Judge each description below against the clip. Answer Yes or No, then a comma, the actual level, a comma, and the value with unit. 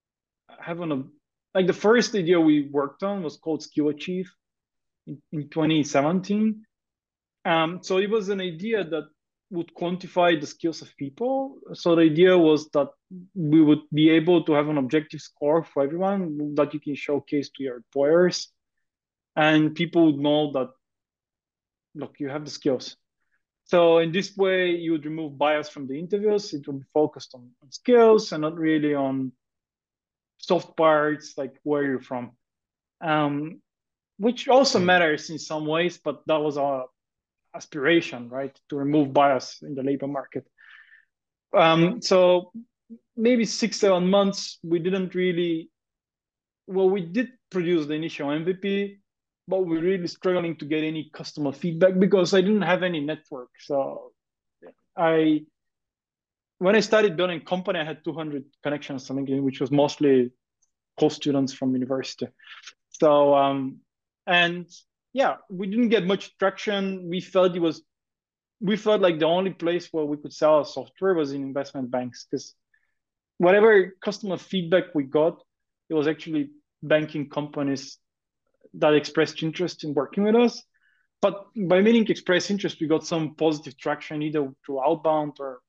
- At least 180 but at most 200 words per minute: No, average, 155 wpm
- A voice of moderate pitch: Yes, medium, 160 Hz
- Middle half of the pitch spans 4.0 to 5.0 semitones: Yes, average, 4.3 semitones